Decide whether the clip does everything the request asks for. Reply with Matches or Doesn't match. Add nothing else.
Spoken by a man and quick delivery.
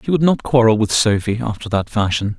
Matches